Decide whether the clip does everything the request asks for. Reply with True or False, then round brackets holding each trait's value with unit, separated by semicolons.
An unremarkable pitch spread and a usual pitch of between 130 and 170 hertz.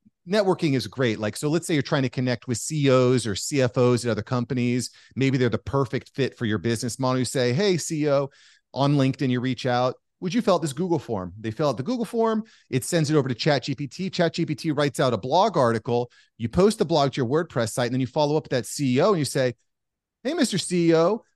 True (4.8 semitones; 135 Hz)